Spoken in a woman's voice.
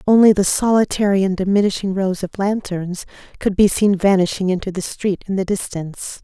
Yes: female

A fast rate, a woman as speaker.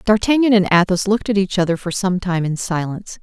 Yes: fast, 225 wpm; female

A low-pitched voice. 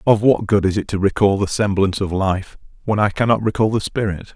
Yes: low, 100 Hz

